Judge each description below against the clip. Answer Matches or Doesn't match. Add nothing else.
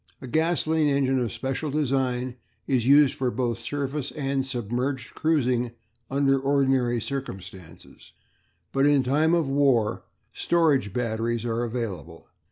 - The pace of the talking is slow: Matches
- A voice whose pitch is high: Doesn't match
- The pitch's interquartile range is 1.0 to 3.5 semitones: Matches